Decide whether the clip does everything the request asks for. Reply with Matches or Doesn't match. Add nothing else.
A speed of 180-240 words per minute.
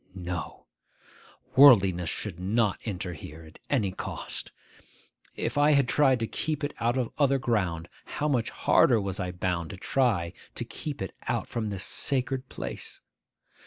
Doesn't match